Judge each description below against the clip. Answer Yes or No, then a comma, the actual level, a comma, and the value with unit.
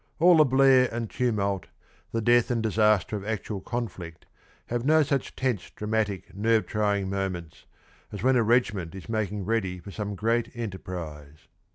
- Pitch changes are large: No, average, 3.6 semitones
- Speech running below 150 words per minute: No, average, 160 wpm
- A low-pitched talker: Yes, low, 105 Hz